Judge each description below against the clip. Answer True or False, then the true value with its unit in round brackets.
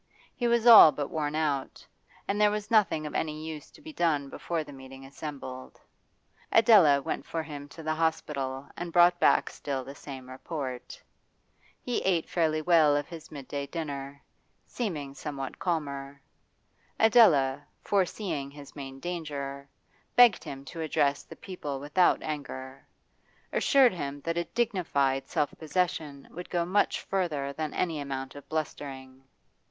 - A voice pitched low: False (150 Hz)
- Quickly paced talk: False (150 wpm)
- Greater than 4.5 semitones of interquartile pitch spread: False (3.9 semitones)